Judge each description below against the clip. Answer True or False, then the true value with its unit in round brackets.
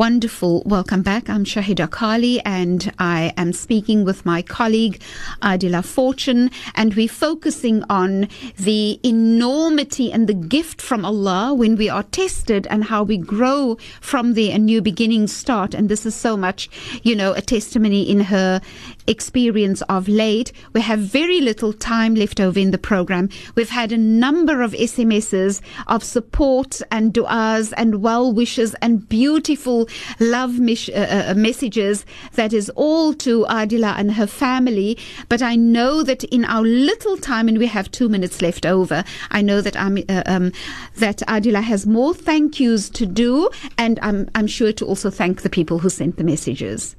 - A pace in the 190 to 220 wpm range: False (170 wpm)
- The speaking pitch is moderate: False (220 Hz)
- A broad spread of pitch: False (3.2 semitones)